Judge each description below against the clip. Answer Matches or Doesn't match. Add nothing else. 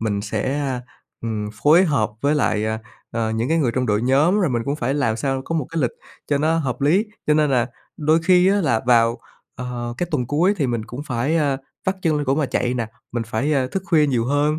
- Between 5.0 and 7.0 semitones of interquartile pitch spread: Doesn't match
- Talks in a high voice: Doesn't match